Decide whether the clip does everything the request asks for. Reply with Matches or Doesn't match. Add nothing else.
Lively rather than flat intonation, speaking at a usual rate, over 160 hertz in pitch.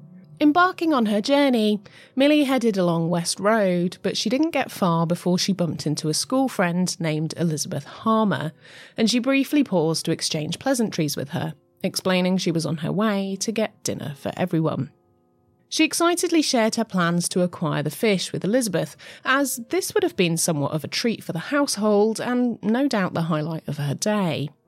Matches